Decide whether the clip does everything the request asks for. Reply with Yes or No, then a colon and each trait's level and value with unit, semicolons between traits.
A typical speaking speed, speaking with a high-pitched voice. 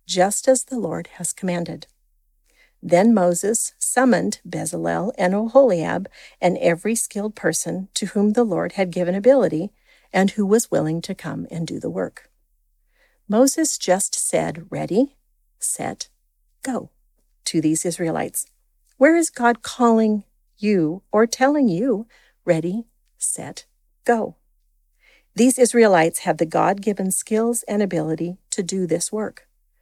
No: slow, 130 wpm; high, 205 Hz